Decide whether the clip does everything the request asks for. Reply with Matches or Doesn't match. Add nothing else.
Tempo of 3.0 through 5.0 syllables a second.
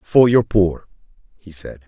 Matches